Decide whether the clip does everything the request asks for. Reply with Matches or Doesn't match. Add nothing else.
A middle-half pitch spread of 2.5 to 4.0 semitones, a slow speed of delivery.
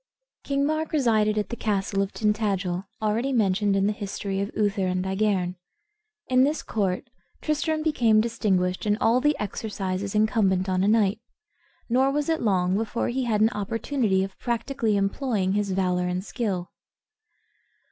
Doesn't match